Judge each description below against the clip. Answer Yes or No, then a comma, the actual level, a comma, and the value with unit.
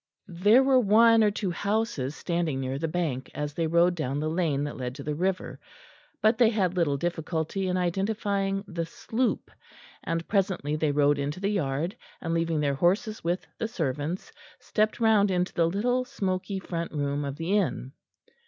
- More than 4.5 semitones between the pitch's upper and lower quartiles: Yes, average, 5.2 semitones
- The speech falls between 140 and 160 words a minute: No, average, 180 wpm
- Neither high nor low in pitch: Yes, medium, 175 Hz